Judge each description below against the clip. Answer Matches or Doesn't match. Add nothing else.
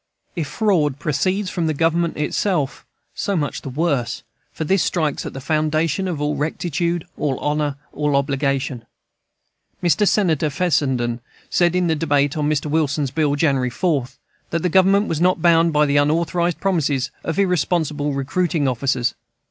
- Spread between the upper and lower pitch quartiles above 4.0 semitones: Doesn't match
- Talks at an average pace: Matches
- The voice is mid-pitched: Matches